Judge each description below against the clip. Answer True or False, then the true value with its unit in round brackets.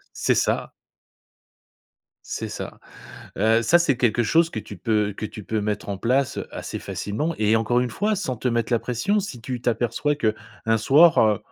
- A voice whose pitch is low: True (115 Hz)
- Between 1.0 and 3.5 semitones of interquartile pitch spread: False (4.3 semitones)